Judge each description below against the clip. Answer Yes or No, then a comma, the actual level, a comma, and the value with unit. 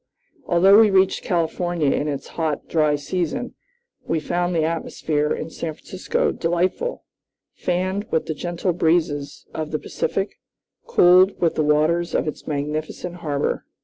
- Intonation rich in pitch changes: No, average, 2.8 semitones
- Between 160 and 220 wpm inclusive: No, average, 145 wpm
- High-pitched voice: No, medium, 170 Hz